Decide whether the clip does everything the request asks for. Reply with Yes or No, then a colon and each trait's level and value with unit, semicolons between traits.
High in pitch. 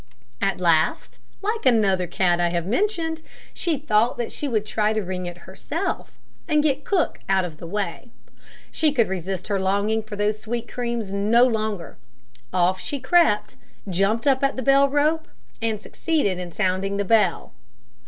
Yes: high, 215 Hz